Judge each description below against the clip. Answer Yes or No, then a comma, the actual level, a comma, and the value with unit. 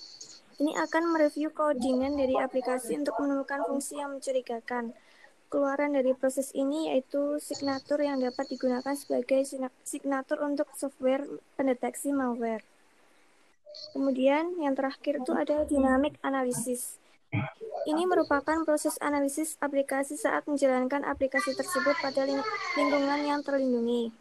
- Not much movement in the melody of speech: Yes, narrow, 1.8 semitones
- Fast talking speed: No, average, 120 wpm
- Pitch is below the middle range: No, very high, 275 Hz